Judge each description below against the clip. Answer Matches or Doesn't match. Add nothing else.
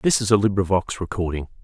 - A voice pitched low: Matches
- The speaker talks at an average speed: Matches